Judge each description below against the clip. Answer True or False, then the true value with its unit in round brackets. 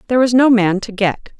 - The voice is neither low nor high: False (220 Hz)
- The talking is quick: True (255 wpm)